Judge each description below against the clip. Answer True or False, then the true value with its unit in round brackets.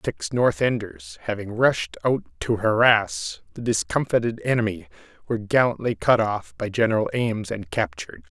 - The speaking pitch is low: True (115 Hz)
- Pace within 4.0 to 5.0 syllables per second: True (4.8 syllables/s)